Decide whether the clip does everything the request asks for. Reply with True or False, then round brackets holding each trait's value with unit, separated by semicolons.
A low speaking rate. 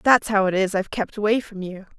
False (270 wpm)